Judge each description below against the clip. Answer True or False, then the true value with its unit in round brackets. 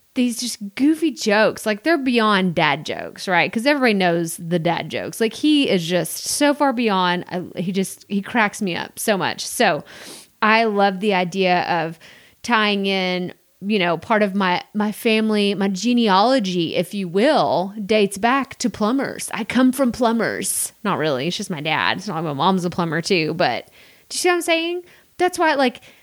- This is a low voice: False (205 Hz)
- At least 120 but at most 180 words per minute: False (195 wpm)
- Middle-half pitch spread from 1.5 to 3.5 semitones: False (5.0 semitones)